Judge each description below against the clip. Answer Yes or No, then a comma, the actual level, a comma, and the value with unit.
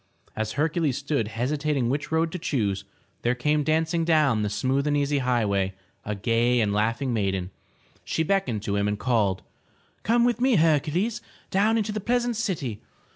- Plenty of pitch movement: Yes, wide, 7.0 semitones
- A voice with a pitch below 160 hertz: Yes, medium, 140 Hz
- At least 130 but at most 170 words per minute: No, average, 180 wpm